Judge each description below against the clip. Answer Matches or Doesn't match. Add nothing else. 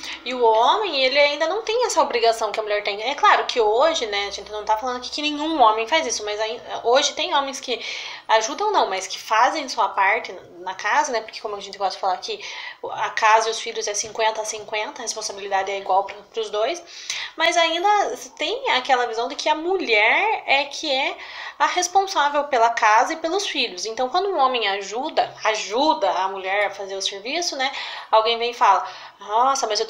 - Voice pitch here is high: Matches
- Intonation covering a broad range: Matches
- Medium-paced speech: Doesn't match